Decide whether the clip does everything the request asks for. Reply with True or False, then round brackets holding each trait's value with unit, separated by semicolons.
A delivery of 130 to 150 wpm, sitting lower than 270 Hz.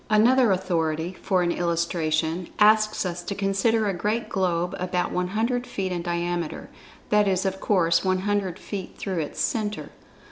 True (145 wpm; 185 Hz)